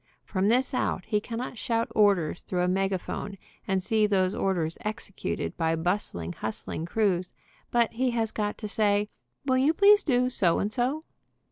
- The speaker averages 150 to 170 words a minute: Yes, average, 165 wpm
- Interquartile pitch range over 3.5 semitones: Yes, average, 4.3 semitones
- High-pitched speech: Yes, high, 210 Hz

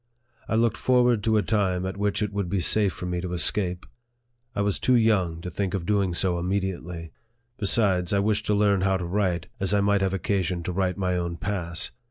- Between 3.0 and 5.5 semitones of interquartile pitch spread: No, narrow, 2.5 semitones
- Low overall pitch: Yes, very low, 95 Hz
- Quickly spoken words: Yes, fast, 220 wpm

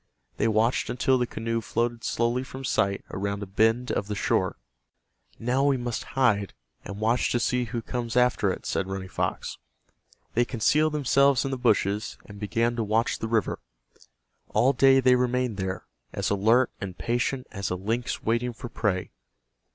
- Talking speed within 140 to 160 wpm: No, average, 175 wpm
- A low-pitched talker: Yes, low, 115 Hz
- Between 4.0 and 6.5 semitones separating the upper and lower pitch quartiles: No, average, 3.3 semitones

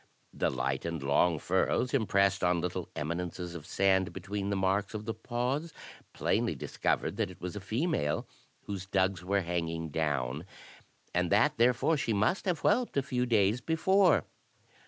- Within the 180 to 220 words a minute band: No, average, 160 wpm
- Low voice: Yes, low, 100 Hz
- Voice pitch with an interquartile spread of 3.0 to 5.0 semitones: No, wide, 5.5 semitones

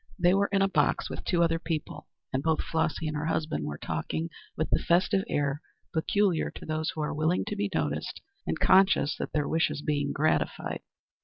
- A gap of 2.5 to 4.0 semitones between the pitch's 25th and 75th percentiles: Yes, average, 2.9 semitones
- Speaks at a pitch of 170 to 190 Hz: No, medium, 160 Hz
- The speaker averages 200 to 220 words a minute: Yes, fast, 205 wpm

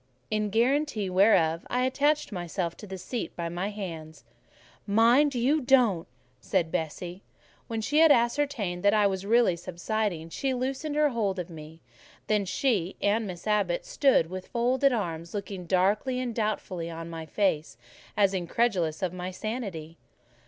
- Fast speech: No, average, 160 wpm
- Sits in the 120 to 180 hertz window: No, high, 200 Hz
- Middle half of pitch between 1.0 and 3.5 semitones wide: No, wide, 5.5 semitones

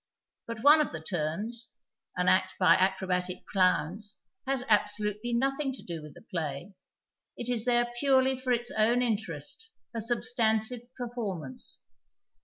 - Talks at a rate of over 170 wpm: No, average, 150 wpm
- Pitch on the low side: No, high, 220 Hz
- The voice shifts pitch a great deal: No, average, 4.9 semitones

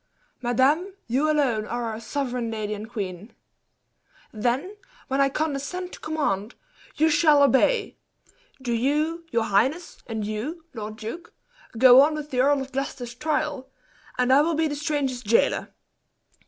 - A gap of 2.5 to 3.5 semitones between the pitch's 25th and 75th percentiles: No, average, 4.7 semitones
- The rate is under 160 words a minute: Yes, average, 150 wpm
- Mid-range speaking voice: No, very high, 270 Hz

